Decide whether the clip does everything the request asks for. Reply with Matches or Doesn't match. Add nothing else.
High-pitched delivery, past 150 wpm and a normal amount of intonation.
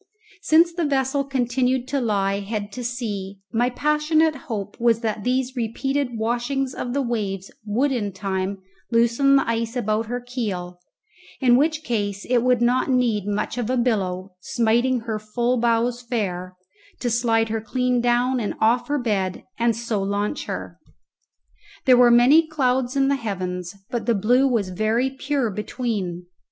Matches